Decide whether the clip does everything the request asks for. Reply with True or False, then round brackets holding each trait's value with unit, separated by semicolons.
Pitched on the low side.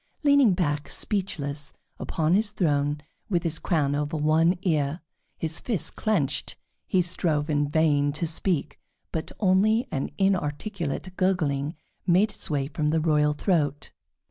False (160 Hz)